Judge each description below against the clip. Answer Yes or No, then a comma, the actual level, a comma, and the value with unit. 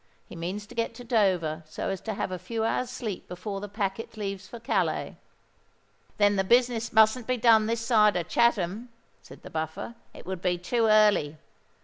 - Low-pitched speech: No, high, 210 Hz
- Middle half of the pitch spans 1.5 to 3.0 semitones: No, average, 3.8 semitones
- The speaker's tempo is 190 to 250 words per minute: Yes, average, 195 wpm